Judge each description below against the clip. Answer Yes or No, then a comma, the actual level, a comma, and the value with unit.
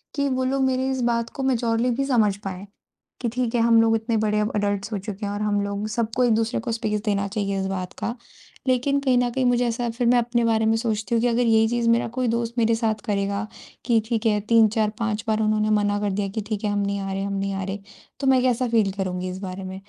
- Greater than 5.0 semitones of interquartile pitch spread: No, average, 2.7 semitones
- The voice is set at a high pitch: Yes, high, 225 Hz